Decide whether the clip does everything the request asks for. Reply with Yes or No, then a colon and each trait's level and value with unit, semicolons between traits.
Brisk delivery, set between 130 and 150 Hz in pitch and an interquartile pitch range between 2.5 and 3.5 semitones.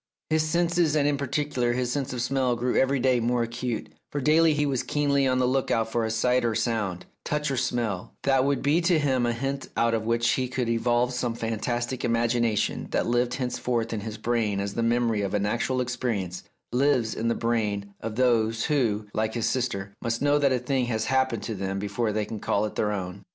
No: fast, 225 wpm; low, 120 Hz; average, 2.8 semitones